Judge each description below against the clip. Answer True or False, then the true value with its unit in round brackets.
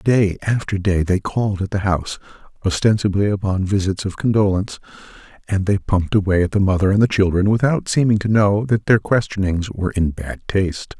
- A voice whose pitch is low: True (100 Hz)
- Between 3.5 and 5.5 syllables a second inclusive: False (5.7 syllables/s)